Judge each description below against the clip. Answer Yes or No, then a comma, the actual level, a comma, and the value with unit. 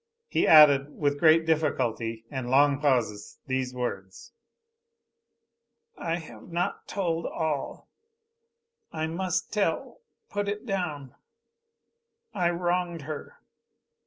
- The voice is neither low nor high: Yes, medium, 155 Hz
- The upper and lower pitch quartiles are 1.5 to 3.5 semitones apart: No, average, 4.7 semitones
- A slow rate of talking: Yes, slow, 100 wpm